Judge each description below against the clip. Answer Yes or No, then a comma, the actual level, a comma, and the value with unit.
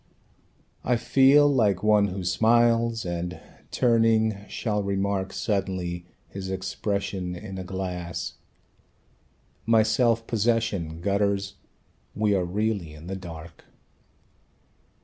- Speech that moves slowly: Yes, slow, 105 wpm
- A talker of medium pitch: No, low, 100 Hz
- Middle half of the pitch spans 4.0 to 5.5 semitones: No, average, 3.3 semitones